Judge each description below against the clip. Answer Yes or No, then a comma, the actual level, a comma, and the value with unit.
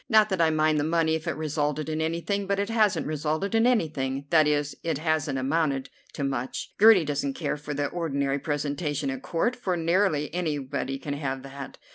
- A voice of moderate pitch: Yes, medium, 155 Hz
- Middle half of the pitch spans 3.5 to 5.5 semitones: No, average, 3.1 semitones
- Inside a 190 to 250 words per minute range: Yes, average, 195 wpm